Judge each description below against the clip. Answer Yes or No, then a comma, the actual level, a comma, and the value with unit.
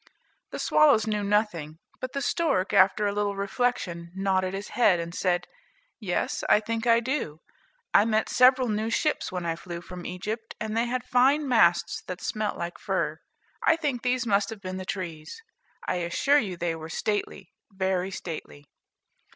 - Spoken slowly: No, average, 175 wpm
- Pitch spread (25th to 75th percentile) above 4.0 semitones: Yes, average, 4.7 semitones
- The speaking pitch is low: No, high, 200 Hz